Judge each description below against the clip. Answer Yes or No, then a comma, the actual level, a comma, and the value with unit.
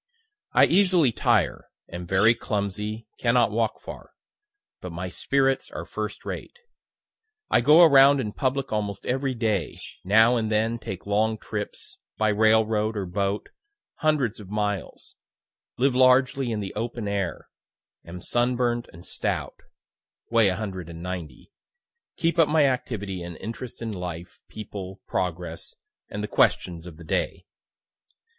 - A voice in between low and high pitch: No, low, 110 Hz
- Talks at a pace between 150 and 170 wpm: No, slow, 135 wpm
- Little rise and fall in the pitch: No, average, 4.5 semitones